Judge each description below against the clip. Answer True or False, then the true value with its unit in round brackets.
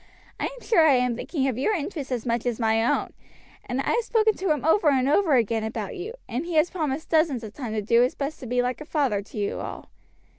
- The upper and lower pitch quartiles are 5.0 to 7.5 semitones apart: True (5.4 semitones)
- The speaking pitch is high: True (270 Hz)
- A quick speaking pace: True (260 wpm)